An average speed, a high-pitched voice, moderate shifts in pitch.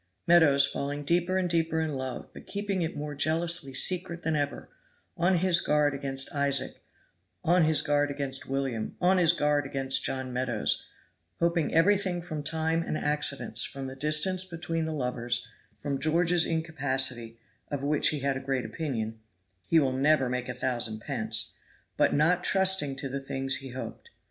No: average, 170 wpm; medium, 145 Hz; average, 3.8 semitones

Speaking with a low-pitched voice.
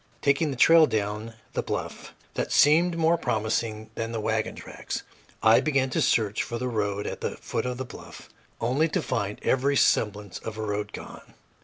Yes: low, 115 Hz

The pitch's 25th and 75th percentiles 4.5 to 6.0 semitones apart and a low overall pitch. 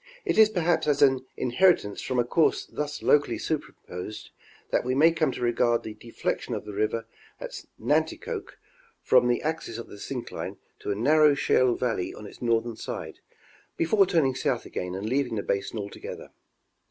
Yes: wide, 5.6 semitones; low, 125 Hz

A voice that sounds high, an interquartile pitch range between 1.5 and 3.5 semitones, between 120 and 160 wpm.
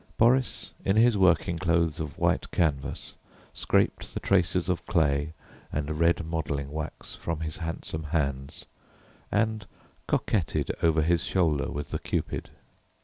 No: very low, 80 Hz; average, 3.2 semitones; slow, 135 wpm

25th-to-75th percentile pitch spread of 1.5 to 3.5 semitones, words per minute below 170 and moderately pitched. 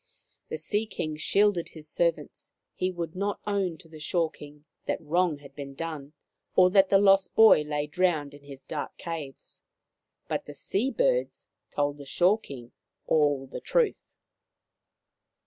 No: average, 4.8 semitones; average, 160 wpm; medium, 165 Hz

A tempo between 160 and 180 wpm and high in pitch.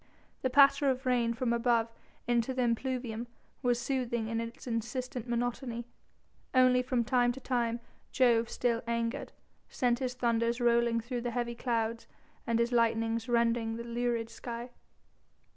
No: average, 150 wpm; high, 235 Hz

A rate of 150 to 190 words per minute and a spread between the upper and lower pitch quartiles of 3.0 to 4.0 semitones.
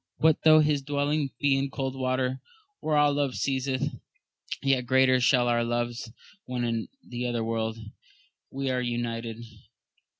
No: average, 160 wpm; narrow, 2.6 semitones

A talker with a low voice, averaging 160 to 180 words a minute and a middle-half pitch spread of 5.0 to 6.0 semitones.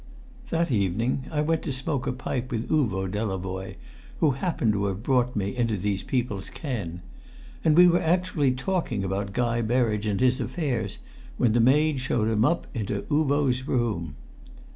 Yes: low, 120 Hz; average, 165 wpm; wide, 5.5 semitones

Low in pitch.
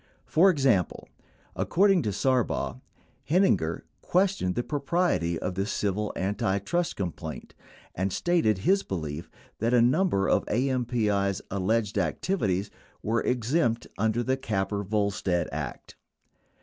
Yes: low, 110 Hz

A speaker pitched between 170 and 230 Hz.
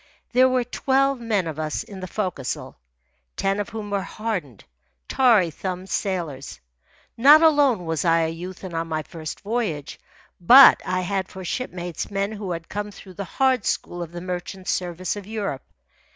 Yes: high, 190 Hz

